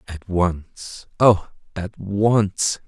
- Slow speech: Yes, slow, 85 wpm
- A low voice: Yes, very low, 95 Hz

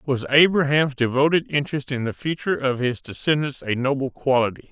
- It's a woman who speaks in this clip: No, male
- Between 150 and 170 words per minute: Yes, average, 165 wpm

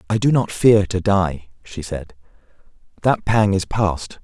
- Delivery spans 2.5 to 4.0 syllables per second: Yes, 3.9 syllables/s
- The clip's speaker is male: Yes, male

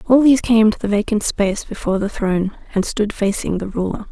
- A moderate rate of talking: No, fast, 220 wpm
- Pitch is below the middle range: No, high, 210 Hz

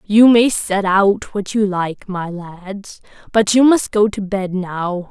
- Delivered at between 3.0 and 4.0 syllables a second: Yes, 3.5 syllables/s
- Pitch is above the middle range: Yes, high, 200 Hz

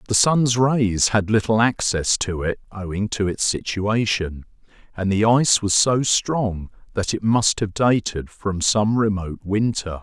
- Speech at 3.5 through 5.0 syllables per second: Yes, 4.1 syllables/s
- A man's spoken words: Yes, male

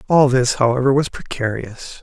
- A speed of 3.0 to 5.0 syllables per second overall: Yes, 4.9 syllables/s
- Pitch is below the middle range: Yes, low, 130 Hz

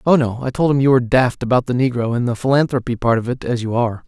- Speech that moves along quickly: Yes, fast, 295 wpm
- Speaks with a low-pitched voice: Yes, low, 125 Hz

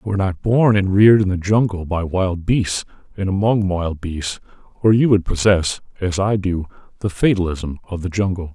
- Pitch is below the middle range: Yes, very low, 95 Hz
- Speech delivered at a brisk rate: No, average, 195 wpm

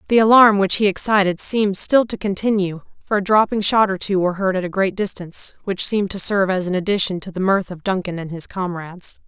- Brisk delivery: Yes, fast, 235 wpm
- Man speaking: No, female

